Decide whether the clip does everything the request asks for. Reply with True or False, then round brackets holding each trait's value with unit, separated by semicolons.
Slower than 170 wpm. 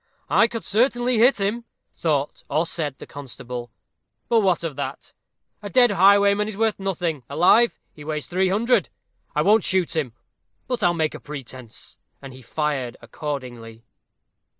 True (150 wpm)